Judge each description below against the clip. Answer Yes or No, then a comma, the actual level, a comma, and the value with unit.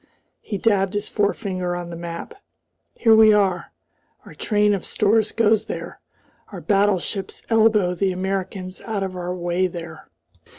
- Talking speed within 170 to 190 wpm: No, average, 145 wpm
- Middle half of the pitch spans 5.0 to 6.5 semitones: No, narrow, 2.6 semitones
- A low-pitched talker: No, high, 195 Hz